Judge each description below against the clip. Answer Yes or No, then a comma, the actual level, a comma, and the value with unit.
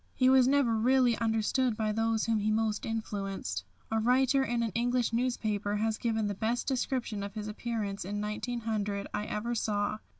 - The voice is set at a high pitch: Yes, high, 225 Hz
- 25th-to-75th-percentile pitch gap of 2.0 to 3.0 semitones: Yes, narrow, 2.4 semitones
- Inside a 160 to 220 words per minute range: Yes, average, 175 wpm